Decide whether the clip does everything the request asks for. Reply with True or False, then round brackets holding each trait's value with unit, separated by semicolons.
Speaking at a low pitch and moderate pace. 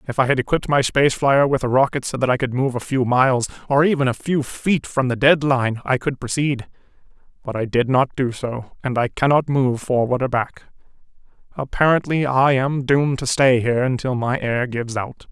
False (130 Hz; 215 wpm)